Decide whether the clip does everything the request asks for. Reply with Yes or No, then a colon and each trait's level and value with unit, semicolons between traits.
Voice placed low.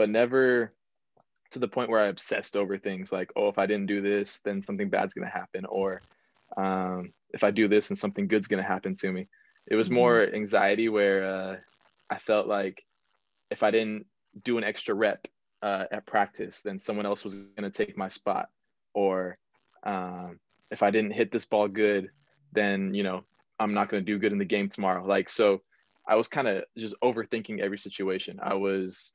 Yes: low, 100 Hz